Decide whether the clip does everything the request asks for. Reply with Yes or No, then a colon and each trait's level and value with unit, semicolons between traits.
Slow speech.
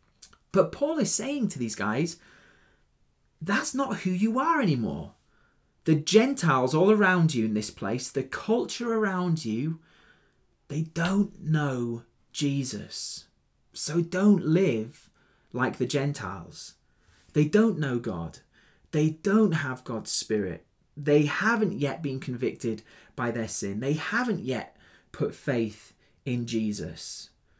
Yes: slow, 130 wpm